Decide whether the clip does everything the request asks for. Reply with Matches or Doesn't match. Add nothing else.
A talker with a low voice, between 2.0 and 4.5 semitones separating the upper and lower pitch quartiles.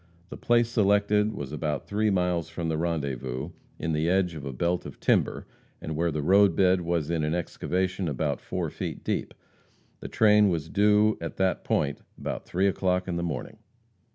Matches